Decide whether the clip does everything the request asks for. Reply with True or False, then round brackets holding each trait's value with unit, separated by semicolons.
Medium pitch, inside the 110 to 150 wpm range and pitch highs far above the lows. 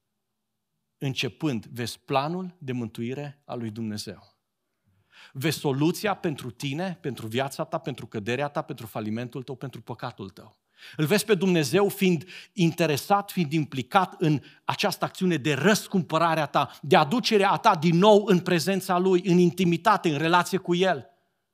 True (160 Hz; 145 wpm; 6.3 semitones)